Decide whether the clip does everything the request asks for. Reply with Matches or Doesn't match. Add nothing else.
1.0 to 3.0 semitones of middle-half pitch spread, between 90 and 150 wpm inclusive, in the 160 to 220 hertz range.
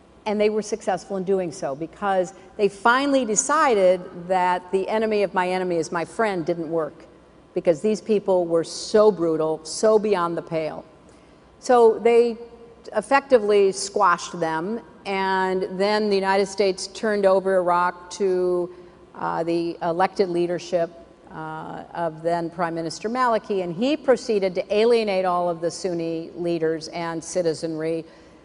Doesn't match